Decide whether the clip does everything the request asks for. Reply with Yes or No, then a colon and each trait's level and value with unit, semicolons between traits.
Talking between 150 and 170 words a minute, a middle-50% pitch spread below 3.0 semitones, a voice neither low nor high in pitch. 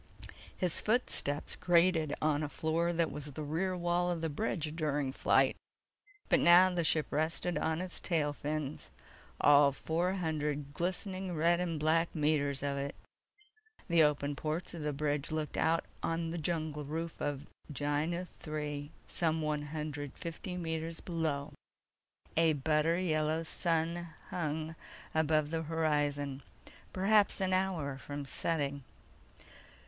No: slow, 135 wpm; narrow, 2.5 semitones; medium, 155 Hz